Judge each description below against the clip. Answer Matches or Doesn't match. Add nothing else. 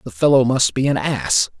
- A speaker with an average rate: Doesn't match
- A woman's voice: Doesn't match